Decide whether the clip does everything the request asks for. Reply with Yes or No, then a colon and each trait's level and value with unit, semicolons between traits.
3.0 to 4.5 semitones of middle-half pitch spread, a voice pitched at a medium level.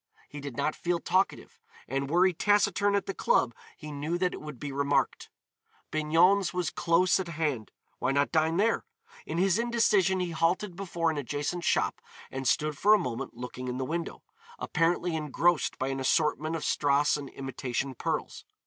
Yes: average, 4.2 semitones; medium, 160 Hz